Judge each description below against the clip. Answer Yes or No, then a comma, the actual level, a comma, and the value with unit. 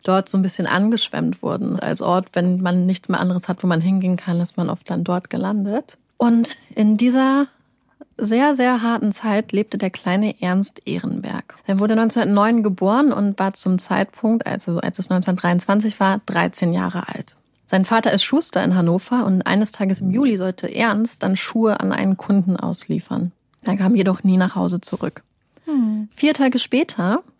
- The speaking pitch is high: Yes, high, 200 Hz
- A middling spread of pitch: Yes, average, 3.6 semitones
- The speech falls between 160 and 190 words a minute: Yes, average, 175 wpm